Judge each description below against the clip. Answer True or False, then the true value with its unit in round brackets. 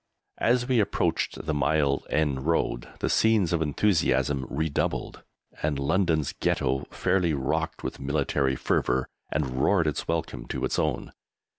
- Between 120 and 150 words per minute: True (140 wpm)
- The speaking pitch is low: True (75 Hz)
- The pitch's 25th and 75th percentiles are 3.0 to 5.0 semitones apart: True (3.7 semitones)